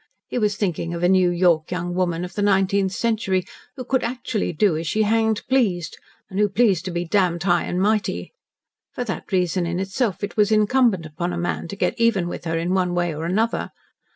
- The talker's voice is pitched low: No, medium, 185 Hz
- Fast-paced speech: Yes, fast, 215 wpm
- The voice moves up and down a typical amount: Yes, average, 3.4 semitones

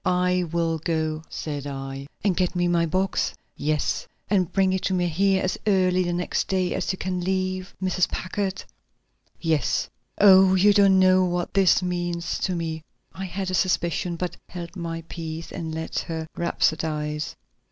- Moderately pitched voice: Yes, medium, 180 Hz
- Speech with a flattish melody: Yes, narrow, 2.3 semitones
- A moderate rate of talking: Yes, average, 170 wpm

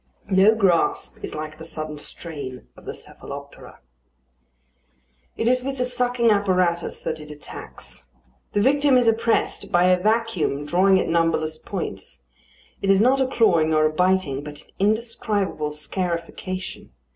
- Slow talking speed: No, average, 145 wpm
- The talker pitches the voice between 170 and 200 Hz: Yes, medium, 185 Hz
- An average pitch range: No, wide, 6.2 semitones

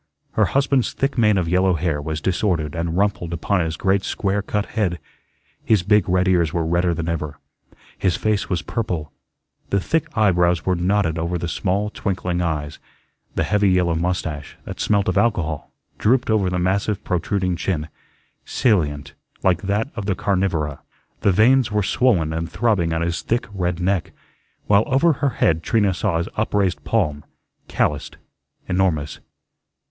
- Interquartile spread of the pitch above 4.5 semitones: No, average, 3.7 semitones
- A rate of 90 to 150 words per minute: No, average, 165 wpm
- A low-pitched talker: Yes, very low, 90 Hz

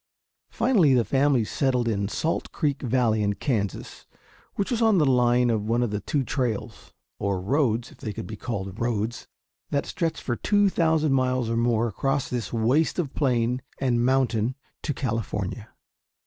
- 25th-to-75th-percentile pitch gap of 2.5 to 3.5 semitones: No, average, 3.9 semitones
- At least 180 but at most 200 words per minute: No, average, 170 wpm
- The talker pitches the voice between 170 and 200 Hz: No, low, 125 Hz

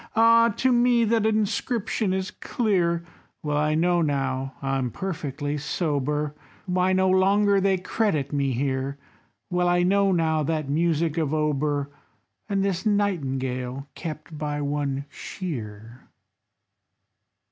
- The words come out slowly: Yes, slow, 125 wpm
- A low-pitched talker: No, medium, 160 Hz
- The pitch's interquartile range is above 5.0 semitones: Yes, wide, 5.4 semitones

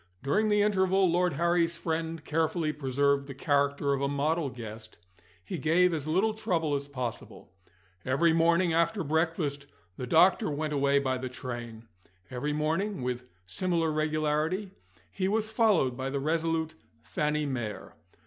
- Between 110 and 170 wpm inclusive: Yes, average, 150 wpm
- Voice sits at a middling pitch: Yes, medium, 155 Hz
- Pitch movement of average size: Yes, average, 3.5 semitones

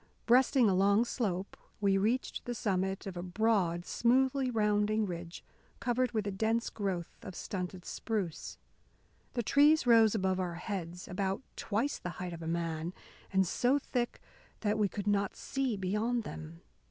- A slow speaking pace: No, average, 160 wpm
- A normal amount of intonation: Yes, average, 4.3 semitones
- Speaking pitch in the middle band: No, high, 205 Hz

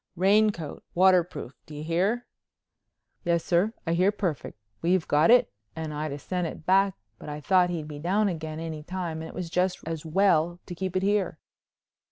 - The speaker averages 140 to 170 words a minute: No, average, 190 wpm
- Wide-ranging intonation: No, average, 2.9 semitones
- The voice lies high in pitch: No, medium, 175 Hz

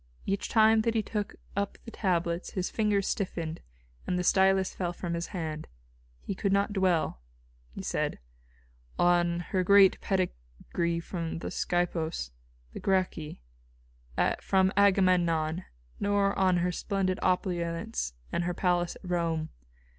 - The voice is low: No, medium, 180 Hz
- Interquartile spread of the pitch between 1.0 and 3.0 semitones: Yes, narrow, 2.5 semitones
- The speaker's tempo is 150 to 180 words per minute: No, slow, 135 wpm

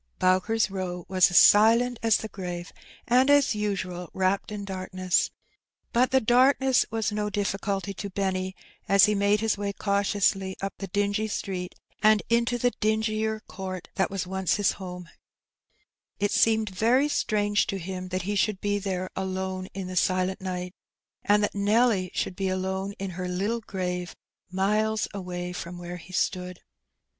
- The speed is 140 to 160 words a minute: No, average, 170 wpm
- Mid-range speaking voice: No, high, 195 Hz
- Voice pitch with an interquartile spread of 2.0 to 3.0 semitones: Yes, narrow, 2.5 semitones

